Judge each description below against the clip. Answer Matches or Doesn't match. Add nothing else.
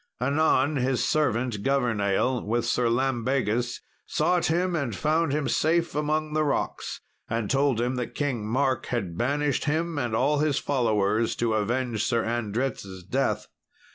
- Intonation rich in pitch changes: Doesn't match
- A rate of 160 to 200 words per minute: Doesn't match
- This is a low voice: Matches